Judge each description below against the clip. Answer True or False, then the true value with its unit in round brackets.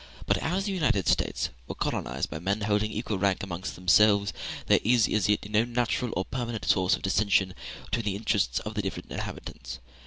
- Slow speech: False (190 wpm)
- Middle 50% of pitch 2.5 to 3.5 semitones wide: True (2.8 semitones)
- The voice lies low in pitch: True (105 Hz)